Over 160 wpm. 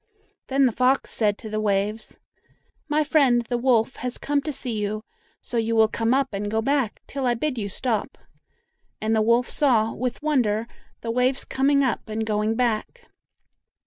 Yes: average, 180 wpm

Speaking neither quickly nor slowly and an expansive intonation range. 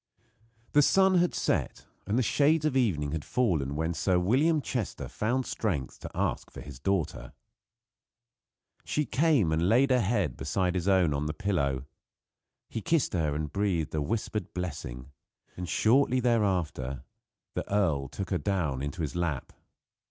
Yes: average, 160 wpm; wide, 8.1 semitones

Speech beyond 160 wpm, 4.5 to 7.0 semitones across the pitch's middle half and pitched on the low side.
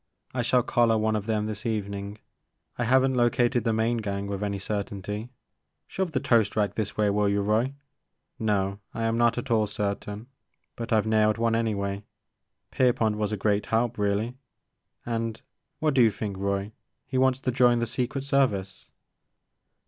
No: average, 190 wpm; average, 2.8 semitones; low, 110 Hz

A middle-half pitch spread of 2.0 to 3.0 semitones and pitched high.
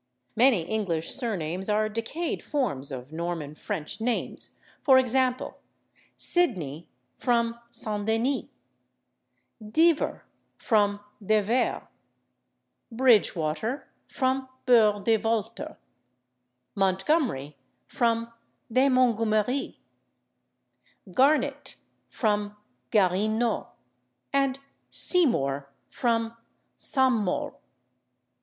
No: average, 4.7 semitones; high, 225 Hz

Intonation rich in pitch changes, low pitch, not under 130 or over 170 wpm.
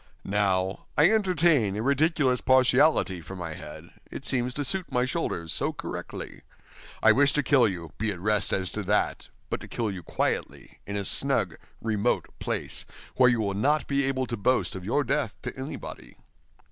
No: wide, 6.0 semitones; low, 120 Hz; average, 185 wpm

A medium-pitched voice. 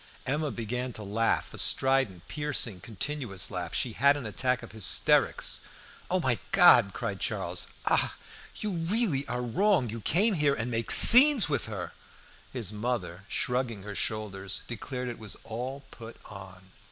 No: low, 120 Hz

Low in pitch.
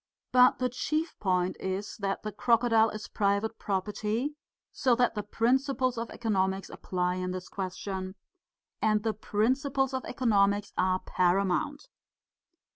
No: high, 210 Hz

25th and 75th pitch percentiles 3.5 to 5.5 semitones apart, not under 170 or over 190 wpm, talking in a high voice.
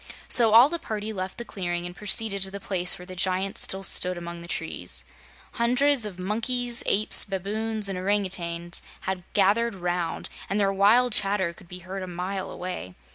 No: average, 3.0 semitones; average, 185 wpm; high, 195 Hz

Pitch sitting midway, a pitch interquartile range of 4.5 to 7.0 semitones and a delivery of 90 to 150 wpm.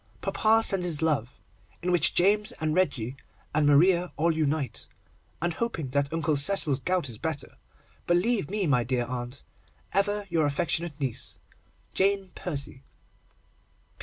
Yes: medium, 160 Hz; average, 4.8 semitones; slow, 135 wpm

